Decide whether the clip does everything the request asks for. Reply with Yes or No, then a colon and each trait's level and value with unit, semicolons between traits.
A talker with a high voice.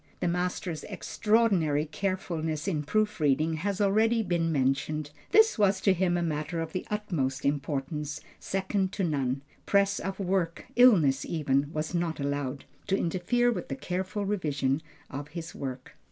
No: medium, 170 Hz